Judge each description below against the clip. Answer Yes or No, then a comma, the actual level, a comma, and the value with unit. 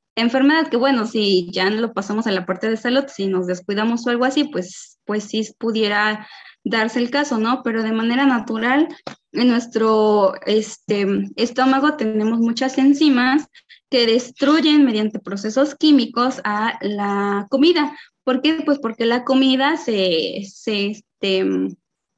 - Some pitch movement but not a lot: Yes, average, 4.2 semitones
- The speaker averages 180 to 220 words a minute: No, average, 150 wpm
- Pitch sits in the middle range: No, high, 230 Hz